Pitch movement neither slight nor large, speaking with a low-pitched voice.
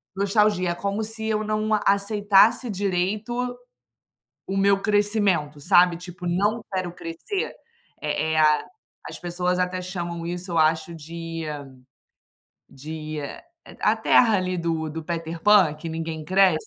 No: average, 3.6 semitones; medium, 180 Hz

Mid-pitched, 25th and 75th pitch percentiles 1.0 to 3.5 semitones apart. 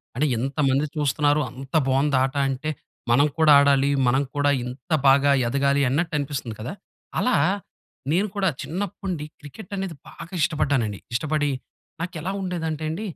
Yes: medium, 145 Hz; average, 3.2 semitones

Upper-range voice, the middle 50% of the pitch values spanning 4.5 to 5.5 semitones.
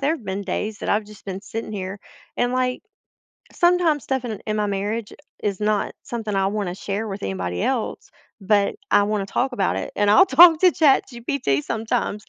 No: high, 210 Hz; average, 3.9 semitones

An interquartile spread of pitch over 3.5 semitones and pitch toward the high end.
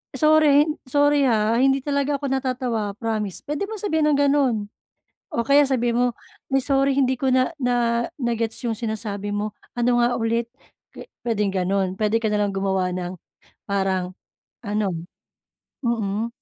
Yes: average, 4.5 semitones; high, 235 Hz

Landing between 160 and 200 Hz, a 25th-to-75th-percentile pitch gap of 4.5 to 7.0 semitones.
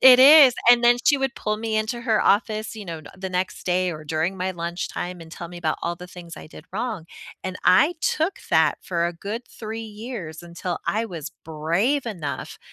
Yes: medium, 185 Hz; average, 5.0 semitones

